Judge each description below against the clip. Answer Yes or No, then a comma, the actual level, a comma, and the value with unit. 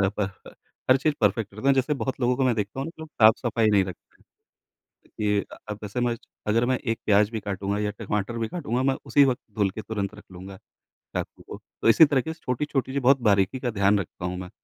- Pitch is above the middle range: No, low, 110 Hz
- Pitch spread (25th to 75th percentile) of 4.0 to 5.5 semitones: Yes, average, 4.4 semitones